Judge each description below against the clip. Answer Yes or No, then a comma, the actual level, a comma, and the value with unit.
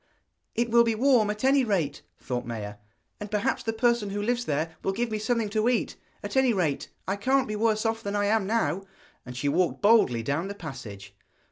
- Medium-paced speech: No, fast, 215 wpm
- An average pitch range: No, wide, 6.2 semitones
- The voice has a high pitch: Yes, high, 210 Hz